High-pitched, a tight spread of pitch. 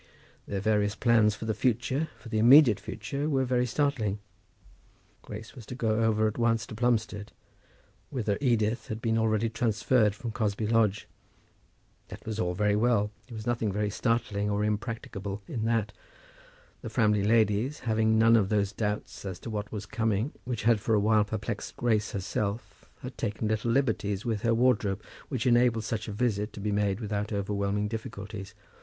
No: low, 110 Hz; narrow, 2.0 semitones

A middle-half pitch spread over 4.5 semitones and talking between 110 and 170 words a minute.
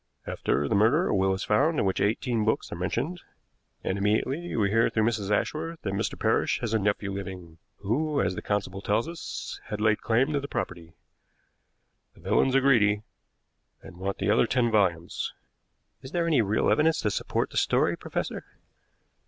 No: wide, 5.5 semitones; average, 185 wpm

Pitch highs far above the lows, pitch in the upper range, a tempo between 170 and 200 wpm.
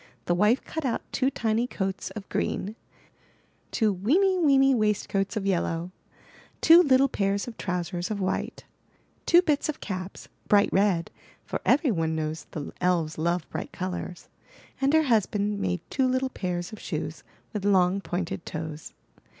No: wide, 5.9 semitones; high, 200 Hz; average, 160 wpm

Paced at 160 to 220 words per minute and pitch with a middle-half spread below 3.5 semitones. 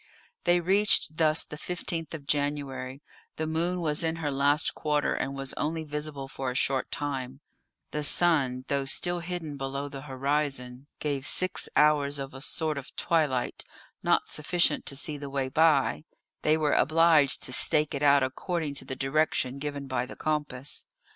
Yes: average, 170 wpm; narrow, 2.6 semitones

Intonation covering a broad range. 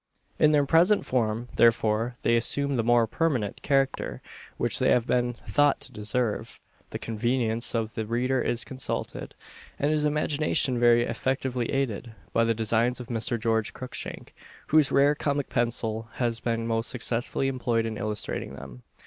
No: average, 2.9 semitones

